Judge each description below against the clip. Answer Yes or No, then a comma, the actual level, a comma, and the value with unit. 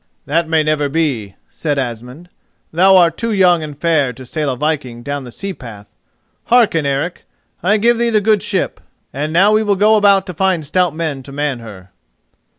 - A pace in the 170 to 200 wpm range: Yes, average, 195 wpm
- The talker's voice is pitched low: No, medium, 160 Hz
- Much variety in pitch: Yes, wide, 5.7 semitones